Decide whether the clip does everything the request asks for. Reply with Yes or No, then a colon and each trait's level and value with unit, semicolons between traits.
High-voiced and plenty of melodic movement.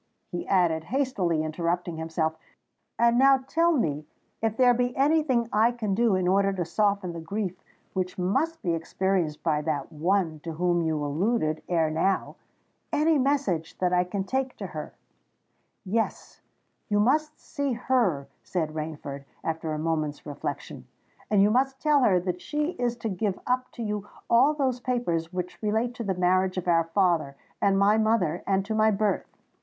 Yes: high, 195 Hz; wide, 6.4 semitones